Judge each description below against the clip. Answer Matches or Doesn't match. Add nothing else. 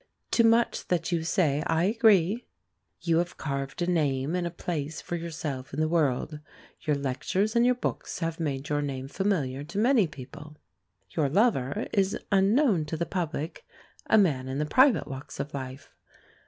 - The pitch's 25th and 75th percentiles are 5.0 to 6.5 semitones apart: Matches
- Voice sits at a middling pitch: Matches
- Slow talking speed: Doesn't match